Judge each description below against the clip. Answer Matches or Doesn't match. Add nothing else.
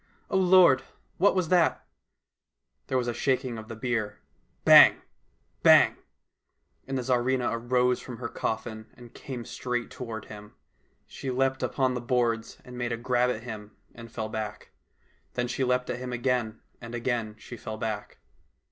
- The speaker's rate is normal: Matches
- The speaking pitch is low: Matches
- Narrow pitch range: Matches